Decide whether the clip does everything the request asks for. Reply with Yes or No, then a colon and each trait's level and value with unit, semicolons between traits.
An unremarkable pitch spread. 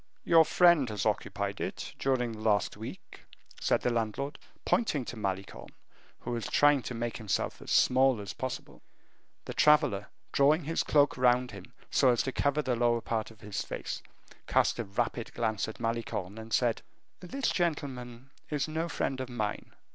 Yes: average, 4.2 semitones